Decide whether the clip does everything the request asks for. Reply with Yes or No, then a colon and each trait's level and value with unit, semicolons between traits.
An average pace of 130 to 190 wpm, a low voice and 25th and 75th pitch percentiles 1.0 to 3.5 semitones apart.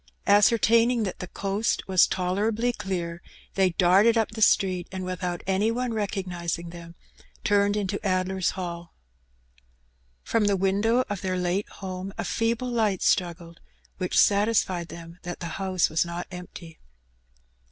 No: average, 145 wpm; high, 190 Hz; average, 2.9 semitones